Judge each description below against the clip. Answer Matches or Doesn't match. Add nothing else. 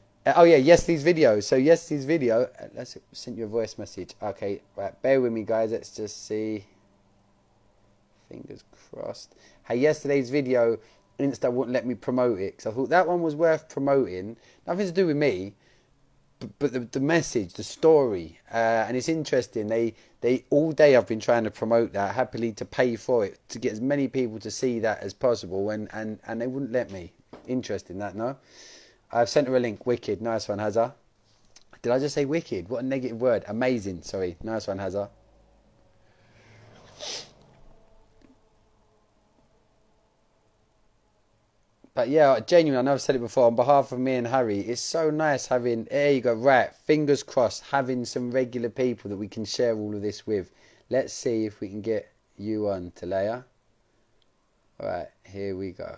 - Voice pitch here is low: Matches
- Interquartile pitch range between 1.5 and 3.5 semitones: Doesn't match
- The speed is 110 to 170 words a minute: Doesn't match